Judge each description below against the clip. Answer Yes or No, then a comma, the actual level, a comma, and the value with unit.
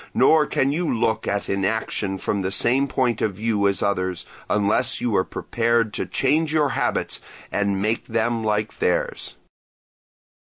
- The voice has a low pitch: Yes, low, 110 Hz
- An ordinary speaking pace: Yes, average, 155 wpm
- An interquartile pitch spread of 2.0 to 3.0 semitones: No, average, 3.9 semitones